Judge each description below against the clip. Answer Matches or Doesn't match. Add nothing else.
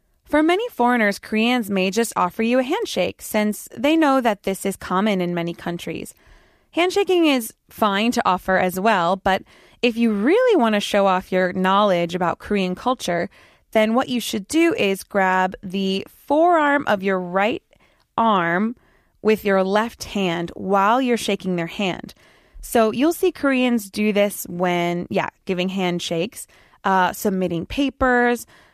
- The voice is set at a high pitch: Matches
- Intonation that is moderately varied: Matches